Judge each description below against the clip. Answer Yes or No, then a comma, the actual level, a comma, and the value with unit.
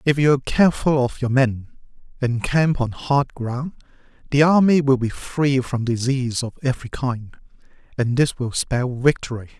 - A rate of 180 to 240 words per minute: No, average, 170 wpm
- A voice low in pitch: Yes, low, 130 Hz